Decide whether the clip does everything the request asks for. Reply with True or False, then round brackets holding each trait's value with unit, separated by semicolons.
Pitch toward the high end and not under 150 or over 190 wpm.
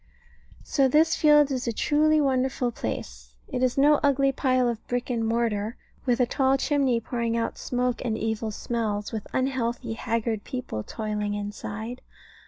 True (240 Hz; 160 wpm)